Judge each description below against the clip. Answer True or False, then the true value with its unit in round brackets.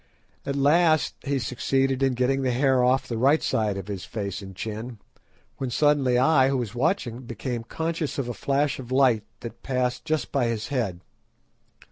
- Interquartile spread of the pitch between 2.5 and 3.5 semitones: True (2.9 semitones)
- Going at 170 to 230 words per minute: True (180 wpm)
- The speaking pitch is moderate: False (130 Hz)